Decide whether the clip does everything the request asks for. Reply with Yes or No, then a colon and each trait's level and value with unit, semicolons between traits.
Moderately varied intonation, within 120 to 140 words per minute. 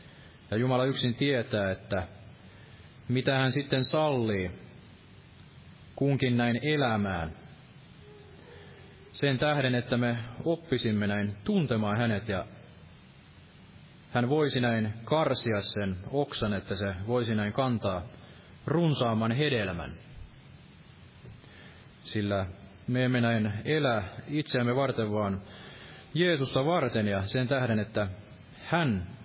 No: average, 4.6 semitones; average, 100 wpm